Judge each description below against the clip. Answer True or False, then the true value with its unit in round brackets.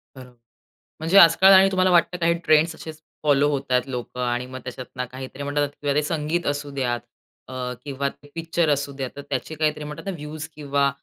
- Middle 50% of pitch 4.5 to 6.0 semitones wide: False (3.1 semitones)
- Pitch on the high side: False (145 Hz)